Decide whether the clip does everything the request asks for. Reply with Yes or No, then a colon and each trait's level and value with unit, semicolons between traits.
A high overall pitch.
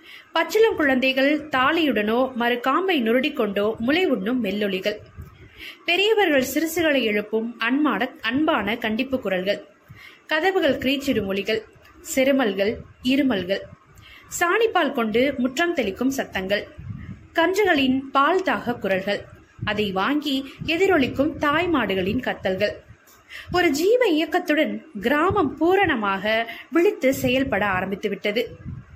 Yes: very high, 265 Hz